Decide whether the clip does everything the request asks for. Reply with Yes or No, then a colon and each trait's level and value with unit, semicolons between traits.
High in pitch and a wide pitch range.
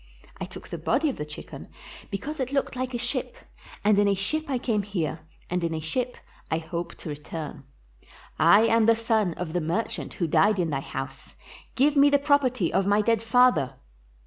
Yes: high, 210 Hz; wide, 7.2 semitones